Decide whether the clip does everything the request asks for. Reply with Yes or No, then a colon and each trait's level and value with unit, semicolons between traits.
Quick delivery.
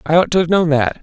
Yes: fast, 350 wpm